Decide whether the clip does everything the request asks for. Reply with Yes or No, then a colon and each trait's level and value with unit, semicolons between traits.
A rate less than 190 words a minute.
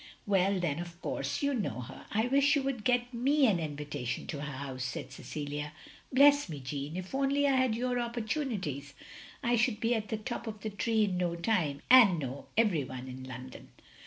No: average, 200 wpm